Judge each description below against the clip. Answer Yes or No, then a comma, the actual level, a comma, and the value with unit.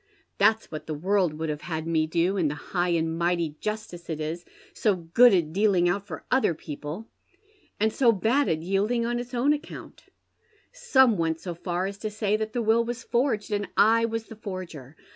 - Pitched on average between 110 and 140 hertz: No, high, 195 Hz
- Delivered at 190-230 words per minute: Yes, average, 200 wpm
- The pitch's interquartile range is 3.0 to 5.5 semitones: Yes, average, 5.2 semitones